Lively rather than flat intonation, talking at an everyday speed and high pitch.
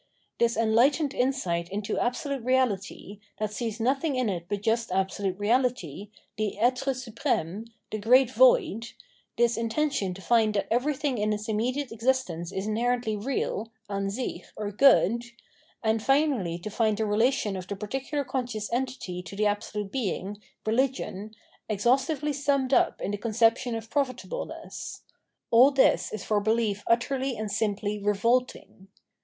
No: average, 4.0 semitones; average, 155 wpm; high, 225 Hz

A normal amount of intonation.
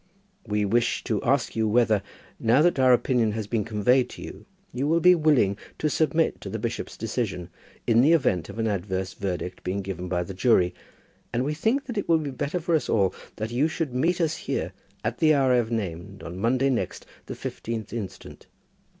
No: wide, 6.4 semitones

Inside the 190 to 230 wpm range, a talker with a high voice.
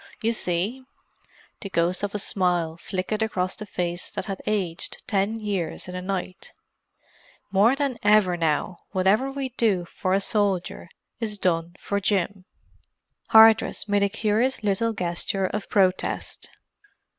No: slow, 135 wpm; high, 195 Hz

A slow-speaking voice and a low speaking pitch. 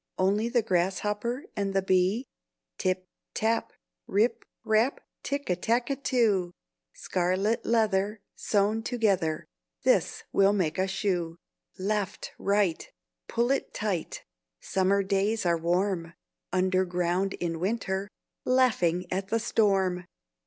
No: slow, 115 wpm; high, 195 Hz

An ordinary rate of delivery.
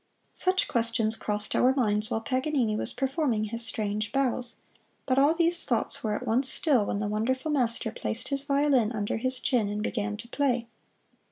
Yes: average, 180 wpm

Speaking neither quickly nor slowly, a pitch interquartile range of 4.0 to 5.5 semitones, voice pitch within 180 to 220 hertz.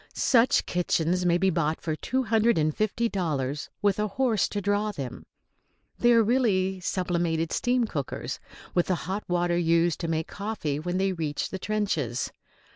Yes: average, 170 wpm; average, 4.5 semitones; medium, 185 Hz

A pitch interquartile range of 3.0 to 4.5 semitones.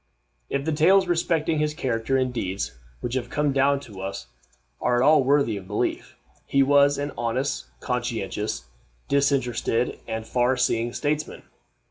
Yes: average, 3.8 semitones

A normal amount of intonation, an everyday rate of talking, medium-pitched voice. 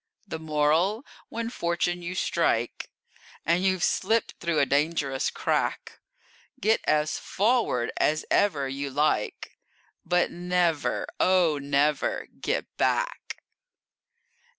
No: average, 4.0 semitones; slow, 105 wpm; medium, 170 Hz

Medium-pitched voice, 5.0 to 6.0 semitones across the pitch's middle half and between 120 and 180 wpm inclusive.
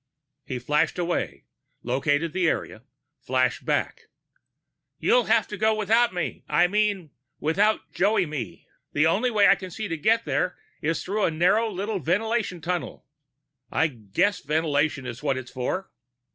Yes: medium, 175 Hz; wide, 5.6 semitones; average, 155 wpm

